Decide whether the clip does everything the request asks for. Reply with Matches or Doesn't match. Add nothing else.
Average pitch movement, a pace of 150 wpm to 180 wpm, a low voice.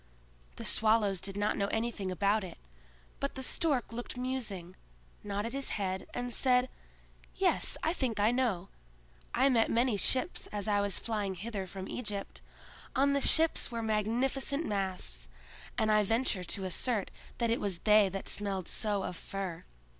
Doesn't match